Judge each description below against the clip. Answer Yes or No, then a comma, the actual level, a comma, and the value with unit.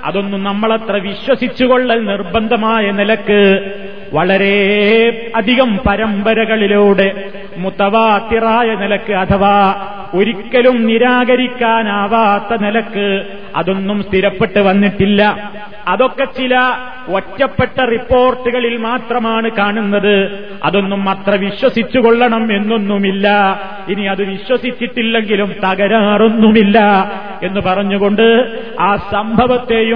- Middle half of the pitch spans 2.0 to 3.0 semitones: Yes, narrow, 2.4 semitones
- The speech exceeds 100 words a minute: No, average, 70 wpm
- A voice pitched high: Yes, high, 205 Hz